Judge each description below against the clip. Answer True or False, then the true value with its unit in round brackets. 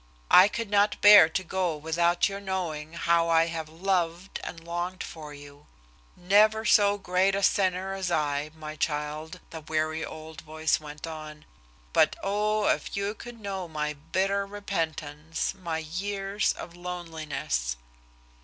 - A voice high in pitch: False (170 Hz)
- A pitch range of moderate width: True (3.9 semitones)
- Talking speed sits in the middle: True (145 wpm)